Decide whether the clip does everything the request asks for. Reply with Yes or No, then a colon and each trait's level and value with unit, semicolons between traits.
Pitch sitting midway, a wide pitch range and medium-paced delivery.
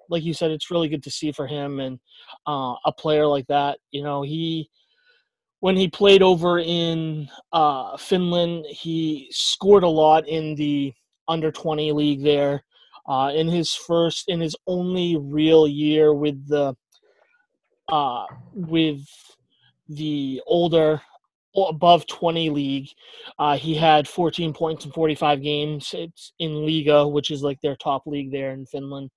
No: medium, 155 Hz; narrow, 2.5 semitones; average, 150 wpm